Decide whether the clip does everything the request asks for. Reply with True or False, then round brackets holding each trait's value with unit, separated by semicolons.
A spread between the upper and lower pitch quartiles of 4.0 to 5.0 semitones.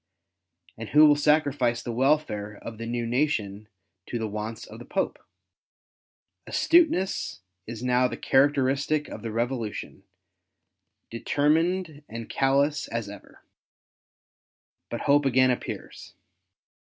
True (4.3 semitones)